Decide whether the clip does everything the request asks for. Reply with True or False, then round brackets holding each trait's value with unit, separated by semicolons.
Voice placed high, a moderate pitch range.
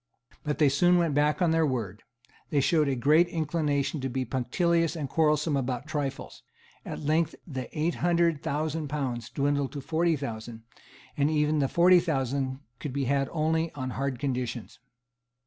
False (145 Hz; 3.3 semitones)